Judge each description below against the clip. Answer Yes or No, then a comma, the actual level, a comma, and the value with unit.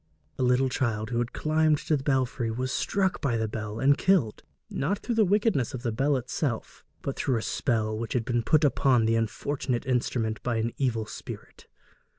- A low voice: Yes, low, 125 Hz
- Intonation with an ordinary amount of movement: Yes, average, 3.9 semitones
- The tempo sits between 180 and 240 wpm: Yes, average, 195 wpm